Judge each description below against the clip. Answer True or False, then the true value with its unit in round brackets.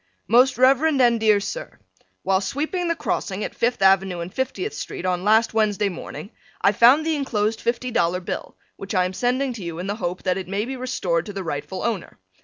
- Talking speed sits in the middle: False (210 wpm)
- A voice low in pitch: False (210 Hz)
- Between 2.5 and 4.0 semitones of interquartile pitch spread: False (5.2 semitones)